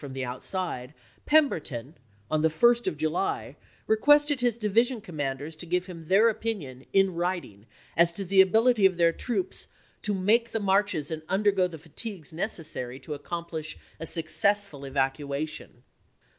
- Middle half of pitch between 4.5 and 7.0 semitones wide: Yes, average, 5.3 semitones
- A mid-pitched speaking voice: Yes, medium, 175 Hz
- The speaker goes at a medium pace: Yes, average, 165 wpm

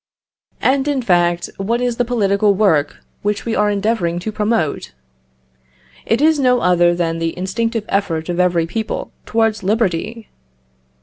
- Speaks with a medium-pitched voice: No, high, 205 Hz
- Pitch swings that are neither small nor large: Yes, average, 4.8 semitones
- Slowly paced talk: No, average, 145 wpm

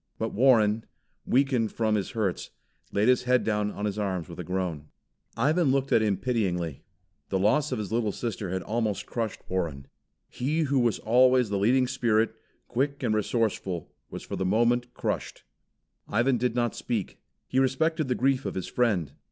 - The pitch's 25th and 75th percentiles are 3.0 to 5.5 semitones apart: Yes, average, 4.2 semitones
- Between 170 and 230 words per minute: Yes, average, 175 wpm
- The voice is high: No, low, 115 Hz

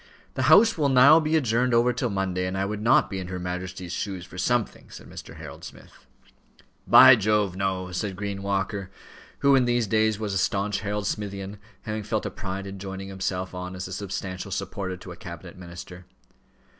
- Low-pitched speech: Yes, low, 100 Hz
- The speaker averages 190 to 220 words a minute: Yes, average, 195 wpm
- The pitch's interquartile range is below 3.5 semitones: Yes, average, 2.9 semitones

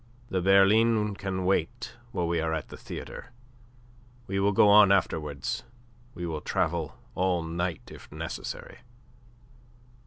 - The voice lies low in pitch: Yes, very low, 95 Hz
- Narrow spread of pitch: No, average, 3.2 semitones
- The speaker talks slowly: Yes, slow, 130 wpm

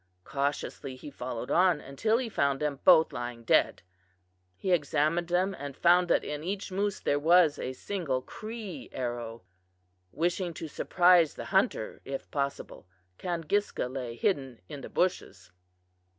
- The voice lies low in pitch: No, medium, 150 Hz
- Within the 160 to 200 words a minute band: No, average, 145 wpm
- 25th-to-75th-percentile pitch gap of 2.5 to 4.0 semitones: No, average, 5.2 semitones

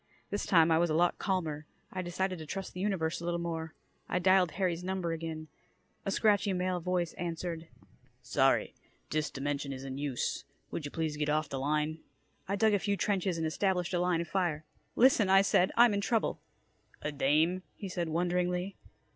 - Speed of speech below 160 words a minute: No, average, 190 wpm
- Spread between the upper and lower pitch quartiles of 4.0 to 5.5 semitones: No, average, 3.1 semitones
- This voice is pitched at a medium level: Yes, medium, 175 Hz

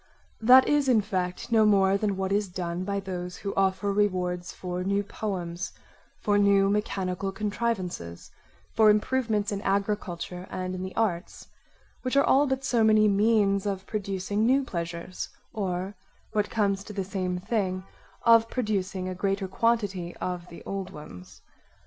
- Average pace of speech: Yes, average, 155 wpm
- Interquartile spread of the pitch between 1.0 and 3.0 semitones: Yes, narrow, 2.6 semitones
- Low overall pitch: No, high, 195 Hz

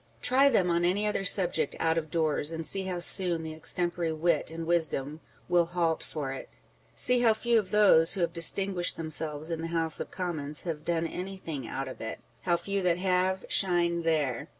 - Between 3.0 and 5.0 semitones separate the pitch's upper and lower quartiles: No, narrow, 2.6 semitones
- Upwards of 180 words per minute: Yes, average, 200 wpm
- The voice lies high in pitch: No, medium, 170 Hz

